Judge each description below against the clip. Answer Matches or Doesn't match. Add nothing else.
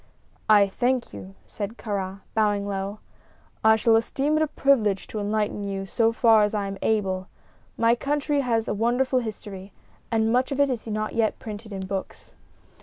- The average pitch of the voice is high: Matches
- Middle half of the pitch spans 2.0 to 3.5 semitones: Matches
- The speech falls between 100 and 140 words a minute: Doesn't match